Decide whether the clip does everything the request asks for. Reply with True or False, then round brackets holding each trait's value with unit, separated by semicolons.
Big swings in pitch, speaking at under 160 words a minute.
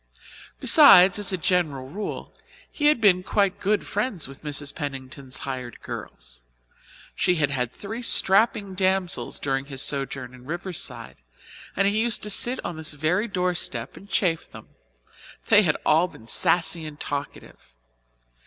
True (6.3 semitones; 150 wpm)